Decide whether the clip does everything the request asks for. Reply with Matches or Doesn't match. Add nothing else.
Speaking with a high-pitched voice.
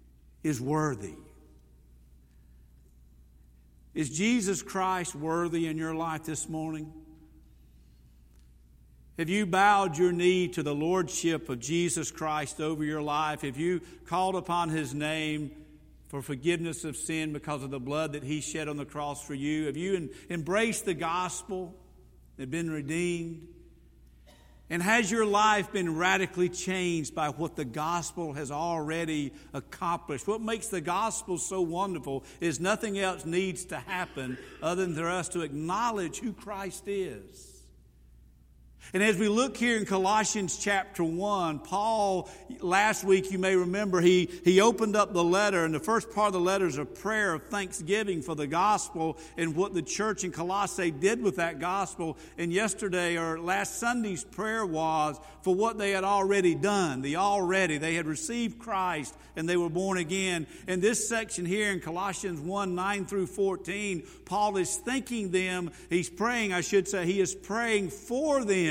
Doesn't match